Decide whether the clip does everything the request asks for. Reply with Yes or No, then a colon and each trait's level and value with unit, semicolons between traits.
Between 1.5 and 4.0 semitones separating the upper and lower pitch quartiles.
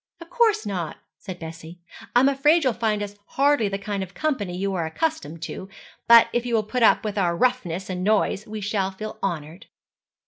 No: average, 5.2 semitones